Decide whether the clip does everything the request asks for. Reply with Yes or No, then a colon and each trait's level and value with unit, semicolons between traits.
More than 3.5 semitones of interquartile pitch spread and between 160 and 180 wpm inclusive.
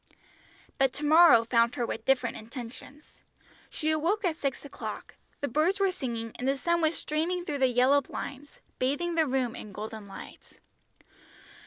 Yes: average, 4.6 semitones; average, 165 wpm